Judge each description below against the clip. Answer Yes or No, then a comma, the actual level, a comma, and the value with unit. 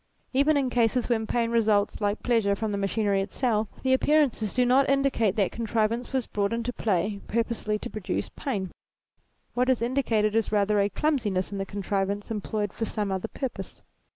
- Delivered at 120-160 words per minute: No, average, 190 wpm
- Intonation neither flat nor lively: Yes, average, 3.3 semitones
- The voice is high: Yes, high, 220 Hz